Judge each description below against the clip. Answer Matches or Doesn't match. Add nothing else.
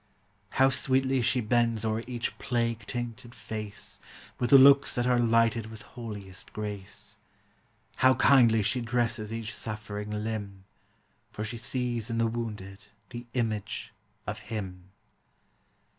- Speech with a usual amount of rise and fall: Doesn't match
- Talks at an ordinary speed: Doesn't match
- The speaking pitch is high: Doesn't match